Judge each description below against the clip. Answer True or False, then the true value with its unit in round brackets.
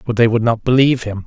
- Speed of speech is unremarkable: False (285 wpm)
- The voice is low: True (115 Hz)